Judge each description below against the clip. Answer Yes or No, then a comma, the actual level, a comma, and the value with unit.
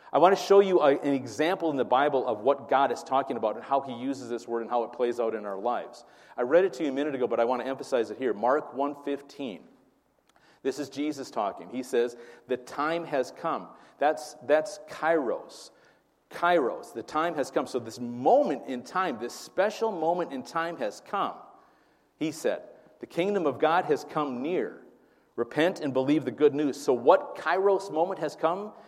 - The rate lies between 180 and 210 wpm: Yes, fast, 205 wpm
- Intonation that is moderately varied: No, wide, 5.7 semitones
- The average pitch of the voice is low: No, medium, 150 Hz